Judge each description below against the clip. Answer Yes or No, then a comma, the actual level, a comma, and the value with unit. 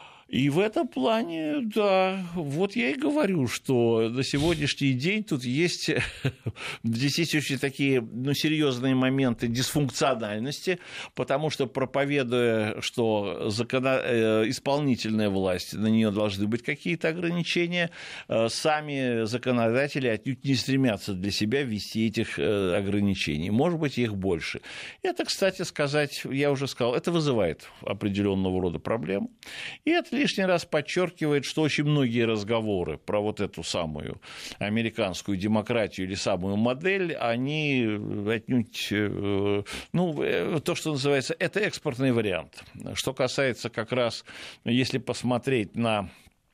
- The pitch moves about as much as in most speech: No, wide, 5.9 semitones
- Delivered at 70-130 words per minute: Yes, average, 120 wpm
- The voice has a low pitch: Yes, low, 130 Hz